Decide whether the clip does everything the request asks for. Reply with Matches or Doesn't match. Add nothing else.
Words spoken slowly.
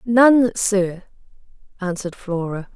Matches